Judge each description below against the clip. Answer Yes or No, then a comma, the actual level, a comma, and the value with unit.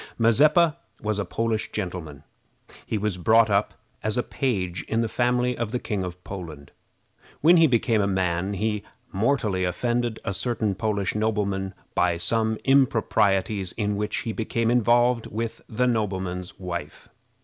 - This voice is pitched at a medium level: No, low, 105 Hz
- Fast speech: No, average, 150 wpm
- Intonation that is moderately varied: Yes, average, 3.7 semitones